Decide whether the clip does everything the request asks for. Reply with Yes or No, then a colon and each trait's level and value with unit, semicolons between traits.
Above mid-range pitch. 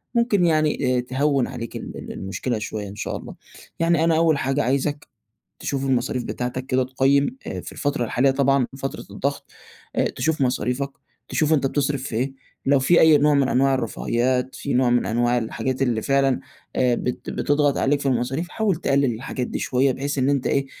No: low, 135 Hz